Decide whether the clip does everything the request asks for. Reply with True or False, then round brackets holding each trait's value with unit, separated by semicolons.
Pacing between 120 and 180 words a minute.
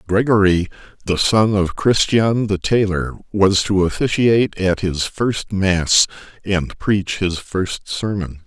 True (135 wpm)